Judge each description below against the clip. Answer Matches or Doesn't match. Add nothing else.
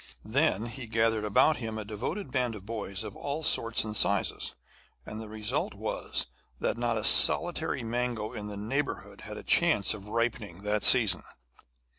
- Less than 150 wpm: Doesn't match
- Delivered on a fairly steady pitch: Matches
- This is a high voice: Doesn't match